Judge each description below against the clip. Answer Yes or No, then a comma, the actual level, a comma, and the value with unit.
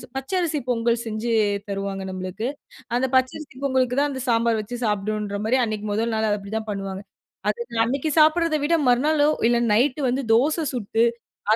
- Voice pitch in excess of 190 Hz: Yes, high, 235 Hz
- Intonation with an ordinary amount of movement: Yes, average, 4.4 semitones